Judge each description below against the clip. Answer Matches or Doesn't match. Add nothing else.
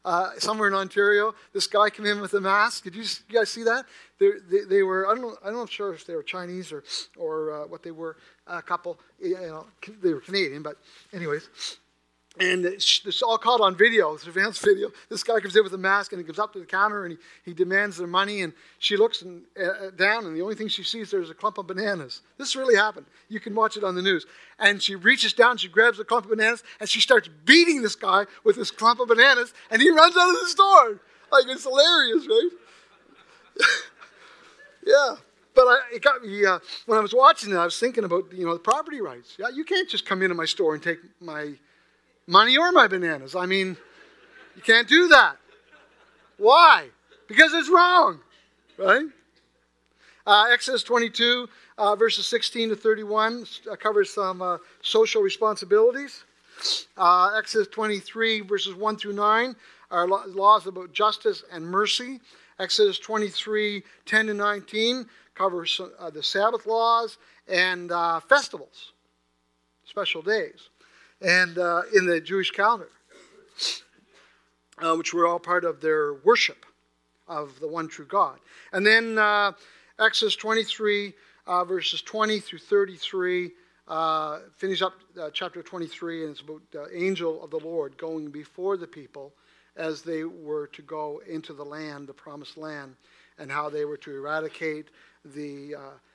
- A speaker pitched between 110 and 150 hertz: Doesn't match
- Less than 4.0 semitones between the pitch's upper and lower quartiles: Doesn't match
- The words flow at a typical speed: Matches